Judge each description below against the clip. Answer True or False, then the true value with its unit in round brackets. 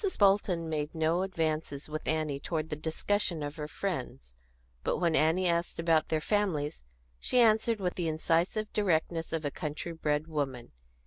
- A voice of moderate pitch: True (160 Hz)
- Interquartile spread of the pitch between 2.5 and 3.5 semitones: True (2.9 semitones)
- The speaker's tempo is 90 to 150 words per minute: False (165 wpm)